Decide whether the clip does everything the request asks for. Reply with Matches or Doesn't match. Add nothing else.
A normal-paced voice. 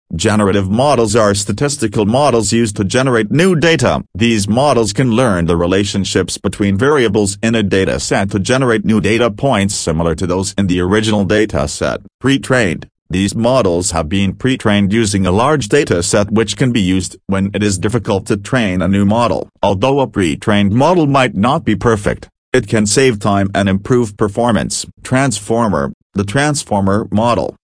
Matches